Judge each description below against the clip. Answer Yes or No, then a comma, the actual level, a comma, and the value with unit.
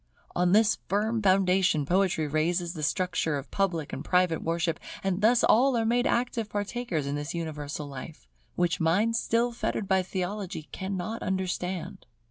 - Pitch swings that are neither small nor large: Yes, average, 4.2 semitones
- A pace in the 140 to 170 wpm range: Yes, average, 155 wpm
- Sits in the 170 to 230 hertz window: Yes, medium, 185 Hz